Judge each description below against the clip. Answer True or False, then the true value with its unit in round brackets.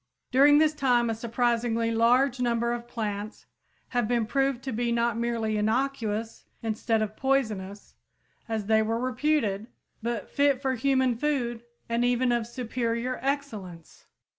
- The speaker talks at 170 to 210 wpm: False (140 wpm)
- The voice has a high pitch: True (235 Hz)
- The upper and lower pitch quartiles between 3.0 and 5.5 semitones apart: False (2.5 semitones)